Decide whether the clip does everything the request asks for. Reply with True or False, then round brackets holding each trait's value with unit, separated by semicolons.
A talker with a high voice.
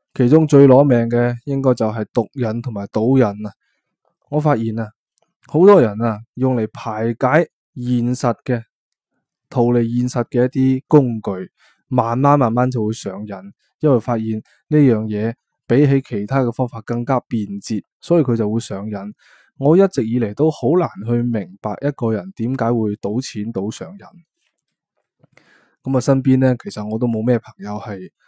False (120 Hz)